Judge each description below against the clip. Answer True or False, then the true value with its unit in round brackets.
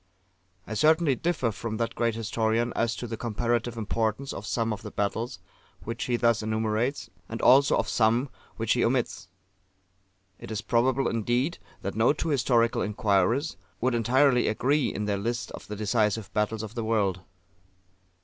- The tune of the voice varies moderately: False (2.2 semitones)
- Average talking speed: True (165 wpm)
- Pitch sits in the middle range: False (115 Hz)